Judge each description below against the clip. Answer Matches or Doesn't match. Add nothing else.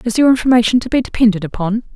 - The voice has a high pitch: Matches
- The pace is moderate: Doesn't match